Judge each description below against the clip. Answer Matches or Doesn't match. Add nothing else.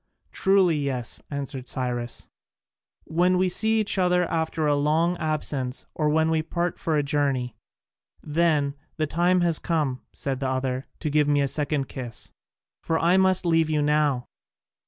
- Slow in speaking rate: Doesn't match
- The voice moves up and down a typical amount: Matches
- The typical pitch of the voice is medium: Matches